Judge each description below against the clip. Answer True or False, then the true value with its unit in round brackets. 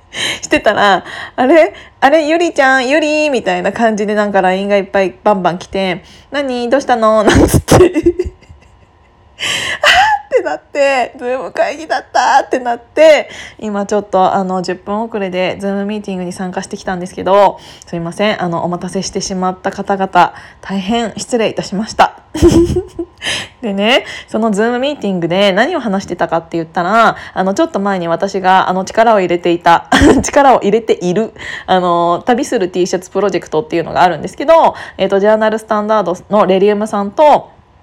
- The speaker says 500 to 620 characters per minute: False (375 characters per minute)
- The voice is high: True (200 Hz)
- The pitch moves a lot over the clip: False (4.7 semitones)